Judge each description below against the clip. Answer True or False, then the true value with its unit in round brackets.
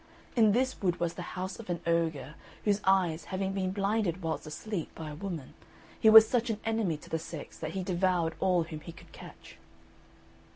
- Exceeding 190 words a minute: True (200 wpm)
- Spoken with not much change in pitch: False (3.7 semitones)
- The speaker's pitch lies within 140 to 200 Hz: True (185 Hz)